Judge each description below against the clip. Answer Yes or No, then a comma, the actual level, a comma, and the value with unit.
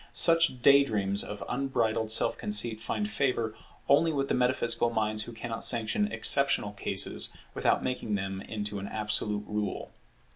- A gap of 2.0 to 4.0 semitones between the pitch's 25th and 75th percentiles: No, average, 4.6 semitones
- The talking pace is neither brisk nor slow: Yes, average, 150 wpm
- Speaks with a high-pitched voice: No, low, 115 Hz